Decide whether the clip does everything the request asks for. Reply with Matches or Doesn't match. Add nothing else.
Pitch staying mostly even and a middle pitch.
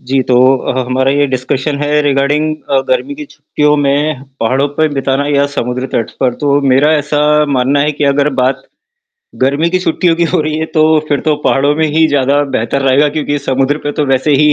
Matches